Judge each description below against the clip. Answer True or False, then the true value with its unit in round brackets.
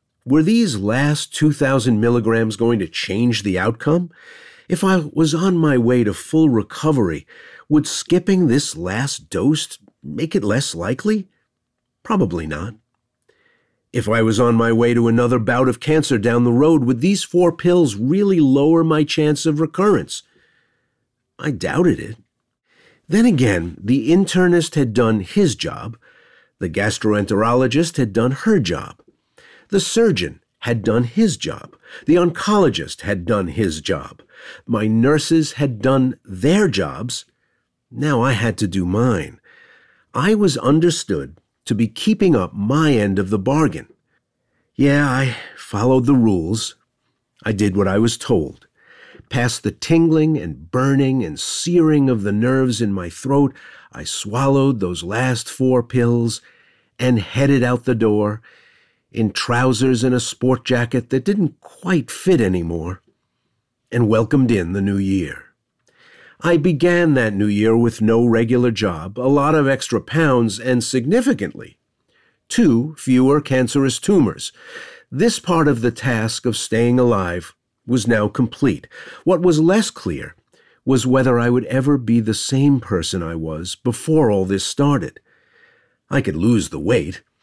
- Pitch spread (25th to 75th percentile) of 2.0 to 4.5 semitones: False (5.3 semitones)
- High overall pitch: False (125 Hz)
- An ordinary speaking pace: True (145 wpm)